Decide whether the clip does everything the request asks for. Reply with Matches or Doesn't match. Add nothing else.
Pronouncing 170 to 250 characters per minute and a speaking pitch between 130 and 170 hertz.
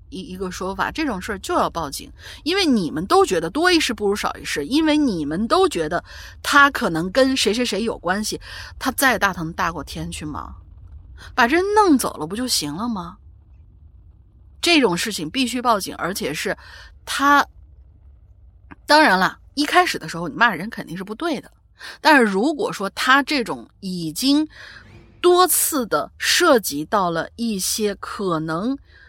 Doesn't match